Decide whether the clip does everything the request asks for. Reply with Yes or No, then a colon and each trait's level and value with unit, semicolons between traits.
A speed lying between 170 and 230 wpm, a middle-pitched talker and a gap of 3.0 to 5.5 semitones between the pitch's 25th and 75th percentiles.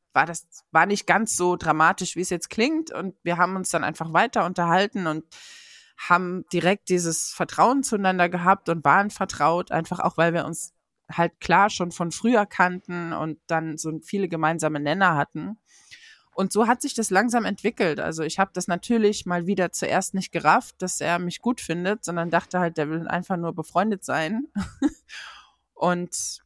Yes: average, 180 wpm; medium, 180 Hz; average, 3.5 semitones